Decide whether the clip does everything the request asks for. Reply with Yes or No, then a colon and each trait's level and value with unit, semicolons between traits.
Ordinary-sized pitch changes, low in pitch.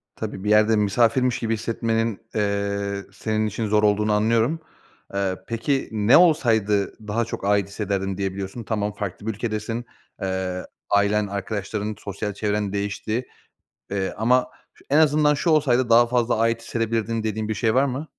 No: narrow, 2.3 semitones; low, 110 Hz